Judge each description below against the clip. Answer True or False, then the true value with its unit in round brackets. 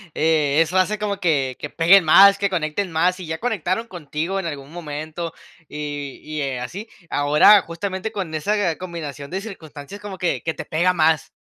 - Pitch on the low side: False (165 Hz)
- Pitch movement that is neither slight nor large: True (4.2 semitones)